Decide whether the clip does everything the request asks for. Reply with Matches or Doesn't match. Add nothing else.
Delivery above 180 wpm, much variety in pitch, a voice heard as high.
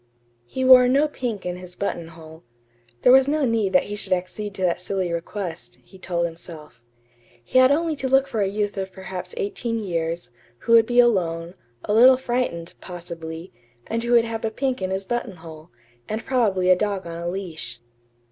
Matches